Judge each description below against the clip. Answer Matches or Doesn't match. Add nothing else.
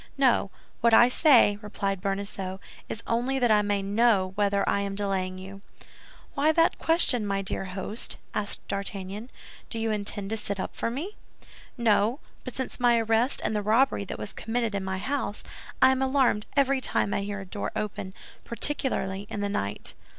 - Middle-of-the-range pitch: Doesn't match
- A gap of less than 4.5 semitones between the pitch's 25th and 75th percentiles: Matches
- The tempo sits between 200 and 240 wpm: Doesn't match